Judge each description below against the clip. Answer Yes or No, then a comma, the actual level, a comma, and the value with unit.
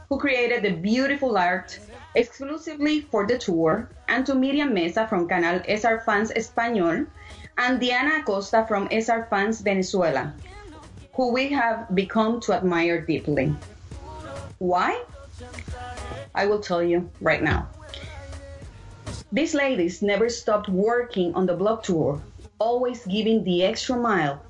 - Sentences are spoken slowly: Yes, slow, 130 wpm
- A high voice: Yes, high, 205 Hz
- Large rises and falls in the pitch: Yes, wide, 5.9 semitones